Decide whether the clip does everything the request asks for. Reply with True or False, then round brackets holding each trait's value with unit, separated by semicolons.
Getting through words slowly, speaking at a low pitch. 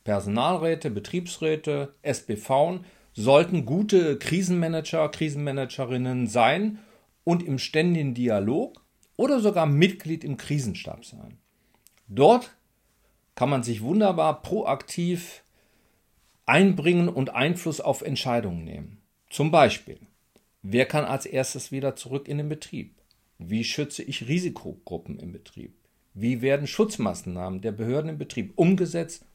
False (110 wpm; 145 Hz)